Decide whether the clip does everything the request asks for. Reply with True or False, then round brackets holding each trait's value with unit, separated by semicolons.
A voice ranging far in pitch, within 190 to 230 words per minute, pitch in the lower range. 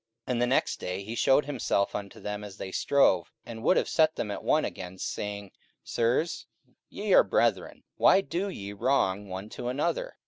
True (5.9 semitones; 195 wpm; 110 Hz)